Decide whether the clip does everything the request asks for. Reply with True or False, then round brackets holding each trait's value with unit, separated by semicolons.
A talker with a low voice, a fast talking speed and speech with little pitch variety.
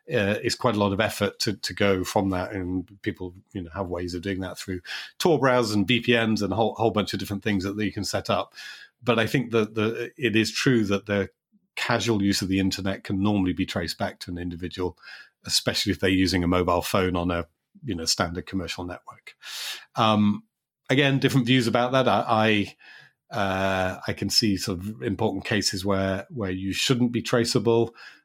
False (100 Hz; 210 wpm; 3.4 semitones)